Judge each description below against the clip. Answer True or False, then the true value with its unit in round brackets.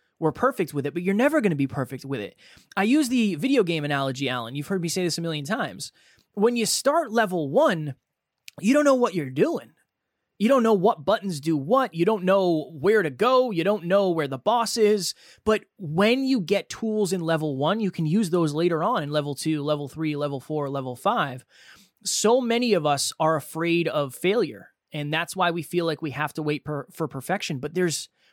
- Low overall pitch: False (170 Hz)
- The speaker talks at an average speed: False (220 wpm)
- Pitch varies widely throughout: True (6.1 semitones)